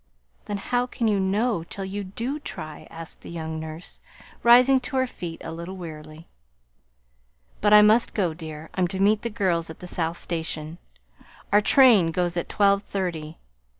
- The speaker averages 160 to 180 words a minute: Yes, average, 175 wpm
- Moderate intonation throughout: Yes, average, 4.3 semitones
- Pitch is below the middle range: No, medium, 185 Hz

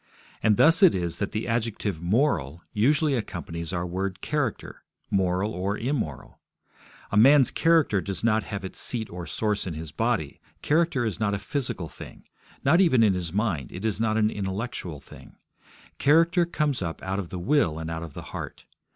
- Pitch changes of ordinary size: No, wide, 6.4 semitones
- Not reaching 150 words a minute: No, average, 185 wpm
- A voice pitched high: No, low, 105 Hz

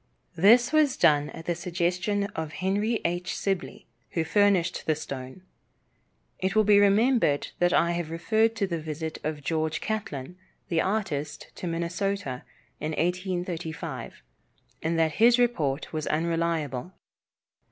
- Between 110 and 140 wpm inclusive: Yes, slow, 135 wpm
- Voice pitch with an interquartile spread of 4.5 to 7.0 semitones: No, average, 4.1 semitones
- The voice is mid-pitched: Yes, medium, 170 Hz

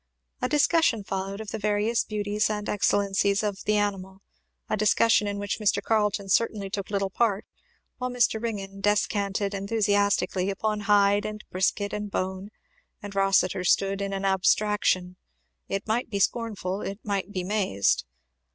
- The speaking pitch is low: No, high, 205 Hz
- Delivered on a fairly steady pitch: Yes, narrow, 1.4 semitones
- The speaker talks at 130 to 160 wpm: Yes, average, 150 wpm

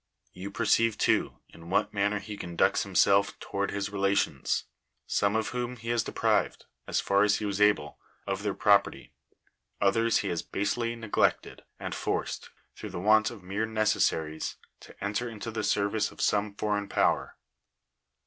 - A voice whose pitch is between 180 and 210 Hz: No, low, 105 Hz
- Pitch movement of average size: No, narrow, 1.7 semitones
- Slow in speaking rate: No, average, 165 wpm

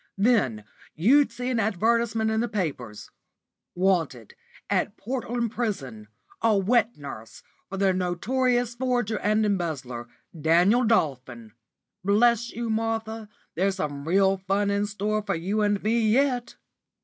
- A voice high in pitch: Yes, high, 205 Hz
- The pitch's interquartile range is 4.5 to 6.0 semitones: Yes, average, 4.9 semitones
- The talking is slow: Yes, slow, 130 wpm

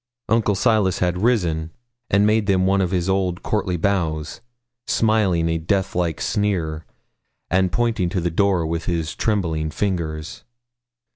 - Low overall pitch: Yes, very low, 90 Hz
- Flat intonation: No, average, 3.5 semitones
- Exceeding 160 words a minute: No, average, 145 wpm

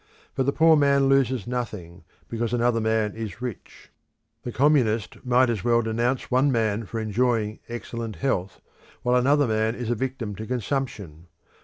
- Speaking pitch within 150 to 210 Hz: No, low, 120 Hz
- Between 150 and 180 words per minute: Yes, average, 160 wpm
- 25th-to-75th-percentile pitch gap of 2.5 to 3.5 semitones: Yes, average, 2.8 semitones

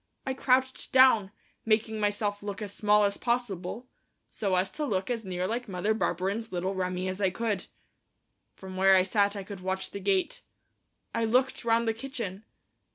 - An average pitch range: Yes, average, 3.3 semitones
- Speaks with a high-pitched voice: Yes, high, 205 Hz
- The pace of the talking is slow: No, average, 175 wpm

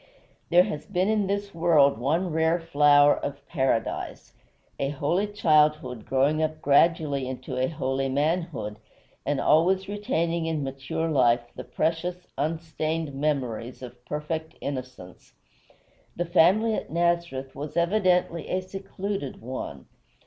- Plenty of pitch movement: No, average, 4.1 semitones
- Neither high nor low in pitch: Yes, medium, 155 Hz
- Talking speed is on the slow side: Yes, slow, 125 wpm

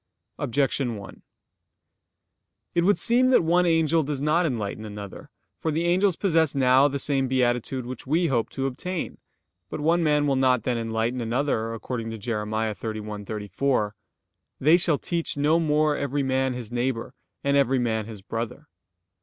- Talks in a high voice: No, low, 135 Hz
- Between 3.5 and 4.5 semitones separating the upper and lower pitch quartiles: No, average, 5.1 semitones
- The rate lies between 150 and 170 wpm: Yes, average, 160 wpm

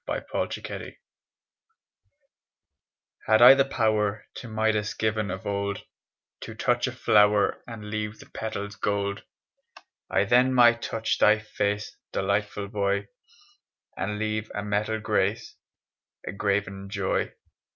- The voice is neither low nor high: No, low, 105 Hz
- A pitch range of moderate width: No, narrow, 1.4 semitones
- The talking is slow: Yes, slow, 125 wpm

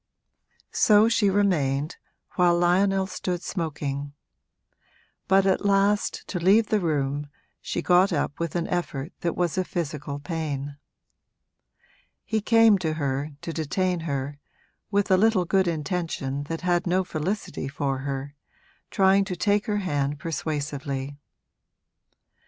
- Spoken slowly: Yes, slow, 130 wpm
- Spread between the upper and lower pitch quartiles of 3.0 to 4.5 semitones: No, average, 4.9 semitones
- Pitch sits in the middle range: Yes, medium, 170 Hz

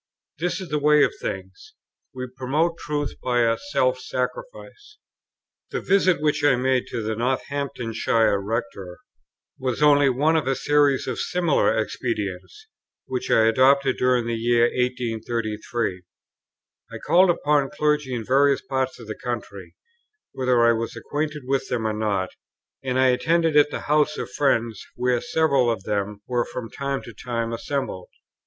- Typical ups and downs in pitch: Yes, average, 4.0 semitones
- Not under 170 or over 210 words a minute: No, average, 155 wpm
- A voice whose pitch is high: No, low, 130 Hz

